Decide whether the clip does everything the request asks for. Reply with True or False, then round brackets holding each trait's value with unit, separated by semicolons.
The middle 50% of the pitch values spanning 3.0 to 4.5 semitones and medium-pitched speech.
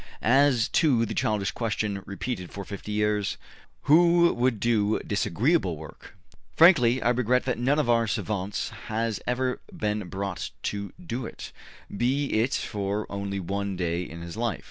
False (4.0 semitones; 110 Hz)